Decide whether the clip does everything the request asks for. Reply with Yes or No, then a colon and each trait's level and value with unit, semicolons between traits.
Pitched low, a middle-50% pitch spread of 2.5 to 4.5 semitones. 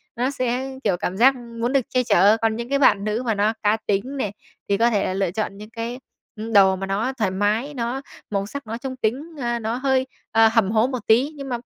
No: high, 230 Hz; average, 3.6 semitones